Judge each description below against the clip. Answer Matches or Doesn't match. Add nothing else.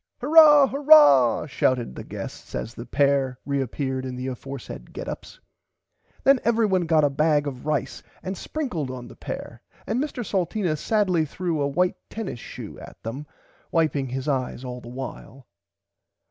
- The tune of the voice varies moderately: Doesn't match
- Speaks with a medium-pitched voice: Matches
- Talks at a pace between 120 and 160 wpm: Matches